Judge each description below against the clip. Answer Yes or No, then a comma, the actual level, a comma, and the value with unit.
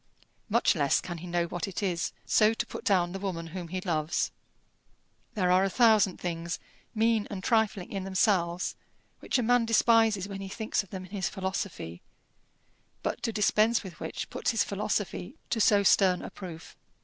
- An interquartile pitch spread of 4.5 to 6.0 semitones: No, average, 3.4 semitones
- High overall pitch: Yes, high, 195 Hz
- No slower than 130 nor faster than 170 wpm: No, average, 185 wpm